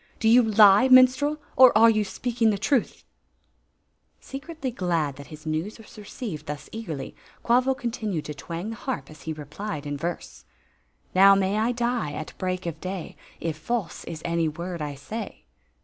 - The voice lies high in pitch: Yes, high, 195 Hz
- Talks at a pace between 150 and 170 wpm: No, average, 190 wpm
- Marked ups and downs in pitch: Yes, wide, 6.7 semitones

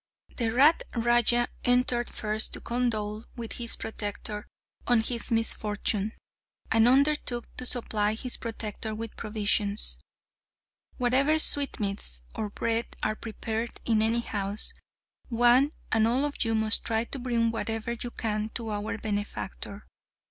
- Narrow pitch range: Yes, narrow, 2.1 semitones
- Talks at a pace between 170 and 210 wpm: No, slow, 135 wpm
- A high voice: Yes, high, 225 Hz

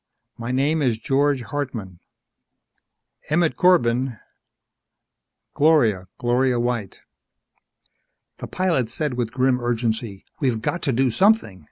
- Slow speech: Yes, slow, 110 wpm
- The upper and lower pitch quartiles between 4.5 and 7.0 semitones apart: No, average, 3.9 semitones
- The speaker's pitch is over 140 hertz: No, low, 125 Hz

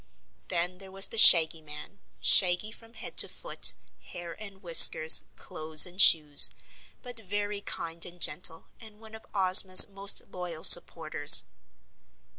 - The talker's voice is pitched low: No, medium, 180 Hz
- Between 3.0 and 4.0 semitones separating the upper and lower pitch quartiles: Yes, average, 3.7 semitones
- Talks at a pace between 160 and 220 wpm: No, average, 140 wpm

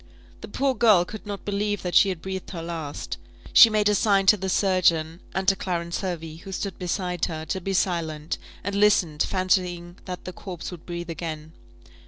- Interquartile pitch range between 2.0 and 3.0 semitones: Yes, narrow, 2.6 semitones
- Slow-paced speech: No, average, 195 wpm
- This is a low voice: No, medium, 185 Hz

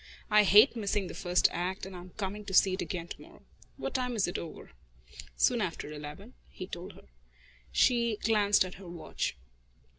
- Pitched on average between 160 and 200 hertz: Yes, high, 190 Hz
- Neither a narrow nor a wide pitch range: Yes, average, 3.0 semitones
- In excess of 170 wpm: Yes, average, 185 wpm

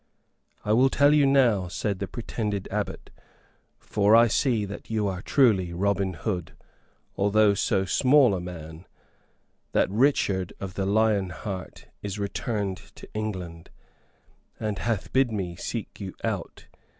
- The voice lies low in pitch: Yes, low, 100 Hz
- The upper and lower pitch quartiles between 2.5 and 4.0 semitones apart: Yes, average, 3.1 semitones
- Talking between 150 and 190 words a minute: No, average, 140 wpm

